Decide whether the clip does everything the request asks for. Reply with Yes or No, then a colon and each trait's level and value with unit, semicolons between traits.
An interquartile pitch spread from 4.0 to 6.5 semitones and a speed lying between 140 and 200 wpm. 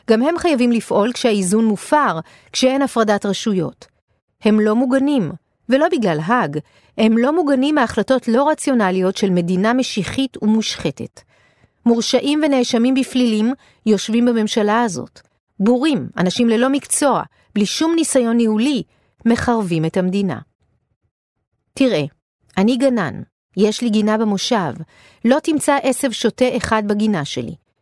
No: average, 4.5 semitones; average, 120 wpm